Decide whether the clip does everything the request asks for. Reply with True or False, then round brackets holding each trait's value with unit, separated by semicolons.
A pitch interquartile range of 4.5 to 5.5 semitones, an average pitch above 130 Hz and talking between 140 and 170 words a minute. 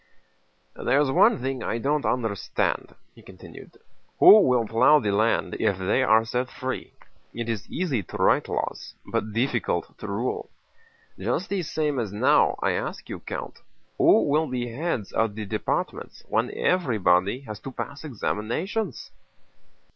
False (4.9 semitones; 125 Hz; 145 wpm)